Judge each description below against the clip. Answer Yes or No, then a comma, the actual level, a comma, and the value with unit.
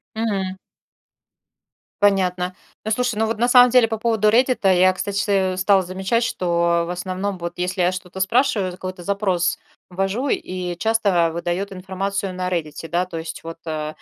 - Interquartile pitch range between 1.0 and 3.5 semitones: Yes, average, 2.9 semitones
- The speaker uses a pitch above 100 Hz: Yes, medium, 185 Hz